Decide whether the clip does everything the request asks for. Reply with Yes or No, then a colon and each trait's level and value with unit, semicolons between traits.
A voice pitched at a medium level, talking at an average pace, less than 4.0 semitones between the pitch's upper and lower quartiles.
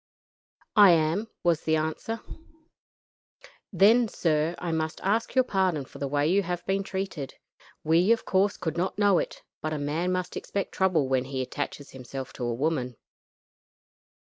No: medium, 165 Hz; average, 165 wpm; average, 4.8 semitones